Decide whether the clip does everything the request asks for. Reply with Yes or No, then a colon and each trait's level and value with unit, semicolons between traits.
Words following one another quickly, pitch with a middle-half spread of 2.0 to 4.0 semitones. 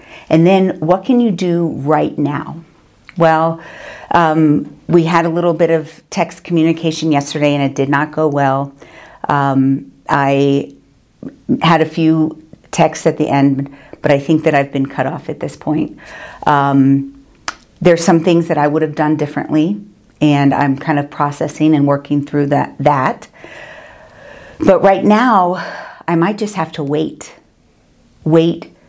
No: average, 155 wpm; average, 2.9 semitones